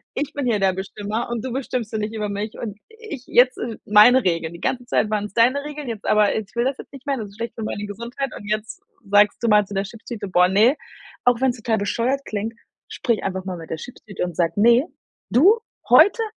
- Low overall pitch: No, high, 225 Hz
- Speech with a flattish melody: No, average, 3.7 semitones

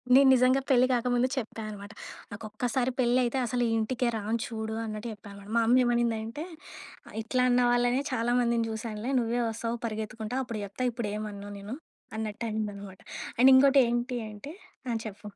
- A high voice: Yes, high, 230 Hz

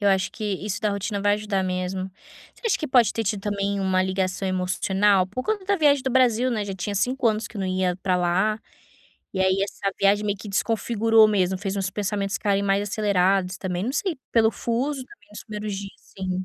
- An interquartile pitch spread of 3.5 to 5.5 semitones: No, average, 2.7 semitones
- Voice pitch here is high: Yes, high, 200 Hz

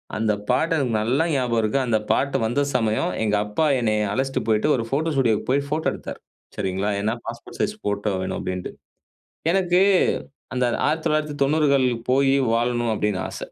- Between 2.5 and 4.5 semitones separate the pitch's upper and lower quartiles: No, average, 4.9 semitones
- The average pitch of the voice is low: Yes, low, 125 Hz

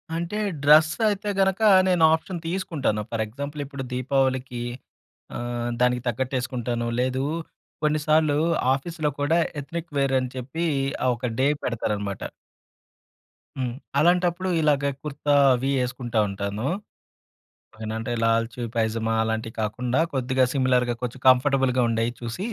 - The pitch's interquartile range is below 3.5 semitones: No, average, 4.1 semitones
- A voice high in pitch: No, low, 130 Hz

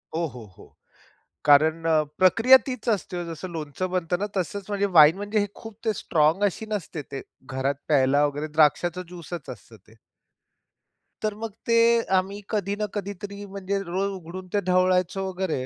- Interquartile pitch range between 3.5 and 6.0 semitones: Yes, average, 4.2 semitones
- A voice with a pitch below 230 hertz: Yes, medium, 185 Hz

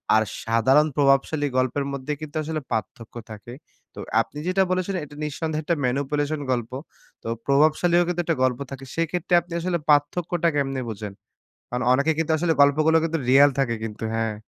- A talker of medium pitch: Yes, medium, 145 Hz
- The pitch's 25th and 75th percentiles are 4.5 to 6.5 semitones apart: No, average, 4.0 semitones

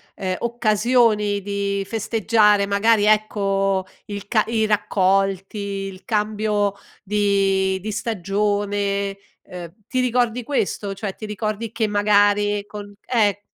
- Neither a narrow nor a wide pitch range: No, narrow, 1.4 semitones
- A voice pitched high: Yes, high, 205 Hz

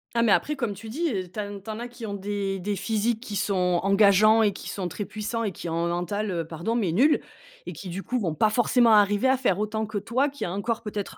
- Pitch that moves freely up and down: No, average, 2.9 semitones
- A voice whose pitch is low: No, high, 210 Hz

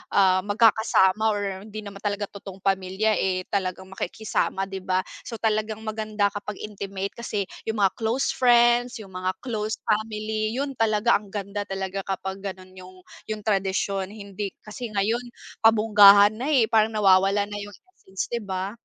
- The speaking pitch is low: No, high, 205 Hz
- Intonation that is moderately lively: No, narrow, 2.2 semitones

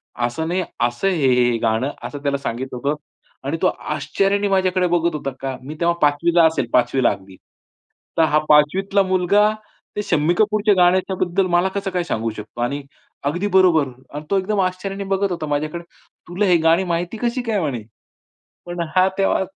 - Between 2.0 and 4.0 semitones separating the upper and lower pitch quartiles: No, average, 4.9 semitones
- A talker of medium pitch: Yes, medium, 170 Hz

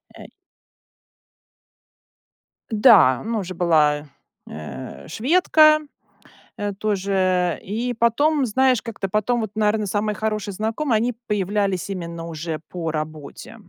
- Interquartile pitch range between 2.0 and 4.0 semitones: No, average, 4.7 semitones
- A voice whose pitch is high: Yes, high, 205 Hz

